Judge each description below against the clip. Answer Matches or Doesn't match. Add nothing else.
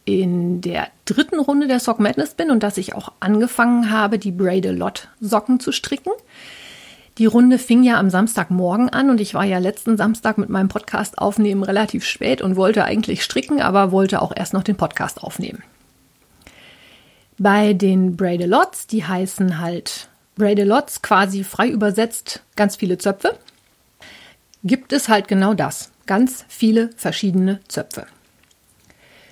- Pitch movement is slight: Doesn't match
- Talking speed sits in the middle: Matches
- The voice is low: Doesn't match